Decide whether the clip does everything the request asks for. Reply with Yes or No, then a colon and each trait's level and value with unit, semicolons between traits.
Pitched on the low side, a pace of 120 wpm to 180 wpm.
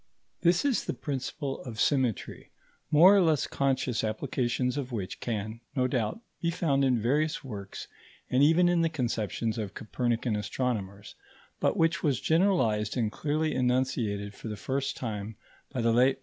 Yes: low, 125 Hz; average, 165 wpm